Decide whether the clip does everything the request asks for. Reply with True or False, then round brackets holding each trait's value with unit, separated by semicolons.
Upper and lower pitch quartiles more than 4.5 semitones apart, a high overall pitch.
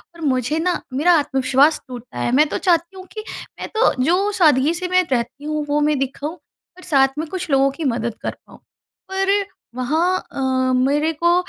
True (4.9 semitones; 300 Hz)